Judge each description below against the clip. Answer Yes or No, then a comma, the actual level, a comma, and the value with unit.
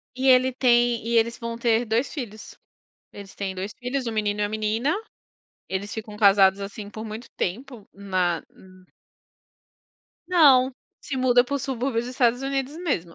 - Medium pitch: No, high, 230 Hz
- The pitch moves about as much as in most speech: Yes, average, 3.9 semitones